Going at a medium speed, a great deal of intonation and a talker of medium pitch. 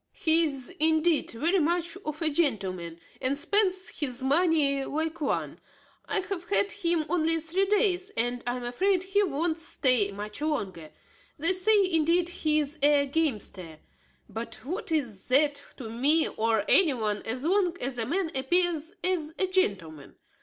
No: average, 160 wpm; wide, 5.7 semitones; very high, 310 Hz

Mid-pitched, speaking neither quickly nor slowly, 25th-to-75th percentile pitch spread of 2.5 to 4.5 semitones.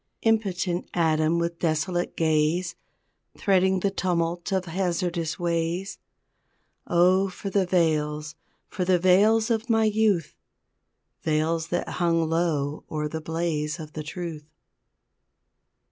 No: medium, 170 Hz; slow, 115 wpm; average, 2.8 semitones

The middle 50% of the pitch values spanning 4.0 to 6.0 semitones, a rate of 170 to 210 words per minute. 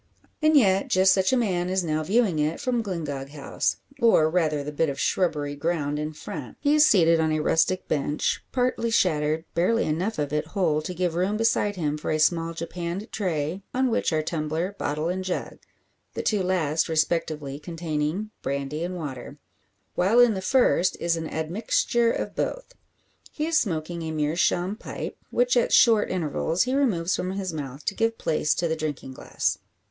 Yes: average, 4.5 semitones; average, 185 wpm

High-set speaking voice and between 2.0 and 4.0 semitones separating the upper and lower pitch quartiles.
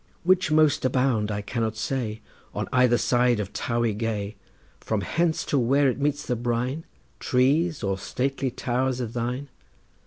No: low, 125 Hz; average, 3.2 semitones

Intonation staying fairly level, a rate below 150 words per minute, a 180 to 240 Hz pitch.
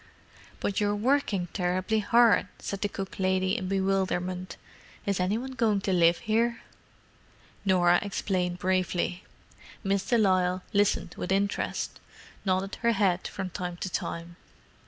Yes: narrow, 2.1 semitones; slow, 135 wpm; high, 190 Hz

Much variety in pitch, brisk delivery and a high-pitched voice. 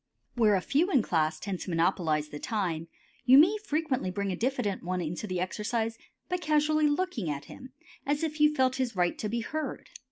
Yes: wide, 8.4 semitones; fast, 210 wpm; high, 225 Hz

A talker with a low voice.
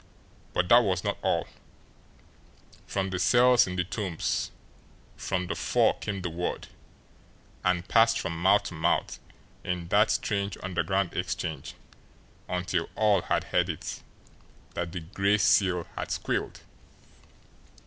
Yes: very low, 90 Hz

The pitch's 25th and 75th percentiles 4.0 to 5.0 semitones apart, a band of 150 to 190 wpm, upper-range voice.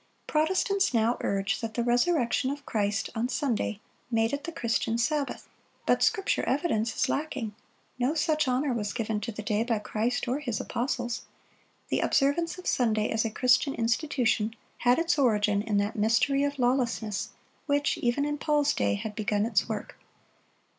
Yes: average, 4.6 semitones; average, 165 wpm; high, 240 Hz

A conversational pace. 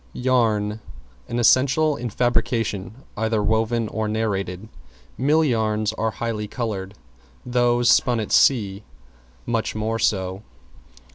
No: slow, 115 wpm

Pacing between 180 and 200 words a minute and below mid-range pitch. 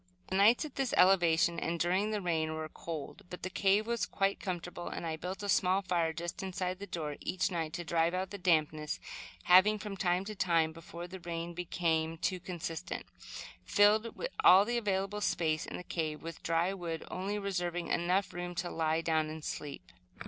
No: average, 190 wpm; medium, 175 Hz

